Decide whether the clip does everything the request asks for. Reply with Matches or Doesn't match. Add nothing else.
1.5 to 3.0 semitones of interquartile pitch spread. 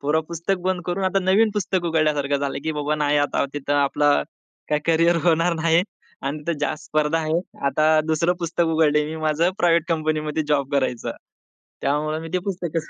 Matches